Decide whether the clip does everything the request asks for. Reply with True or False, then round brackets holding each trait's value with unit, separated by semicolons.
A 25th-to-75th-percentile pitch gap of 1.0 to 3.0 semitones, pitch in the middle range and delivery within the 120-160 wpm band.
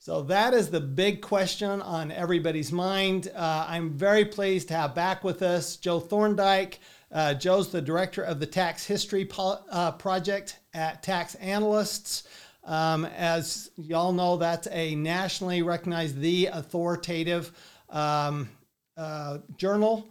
True (2.7 semitones; 175 Hz; 140 wpm)